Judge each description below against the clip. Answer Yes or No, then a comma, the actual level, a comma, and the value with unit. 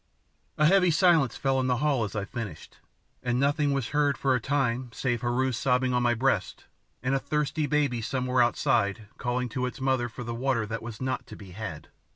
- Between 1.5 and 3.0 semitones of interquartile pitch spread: Yes, average, 2.7 semitones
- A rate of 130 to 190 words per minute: No, fast, 205 wpm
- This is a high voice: No, low, 125 Hz